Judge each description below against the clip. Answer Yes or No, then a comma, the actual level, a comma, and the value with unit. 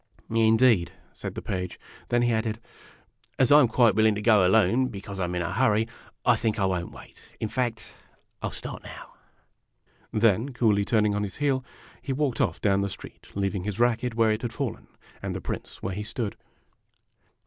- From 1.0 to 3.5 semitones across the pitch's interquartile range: Yes, average, 3.2 semitones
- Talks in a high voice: No, low, 110 Hz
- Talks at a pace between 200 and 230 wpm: Yes, fast, 205 wpm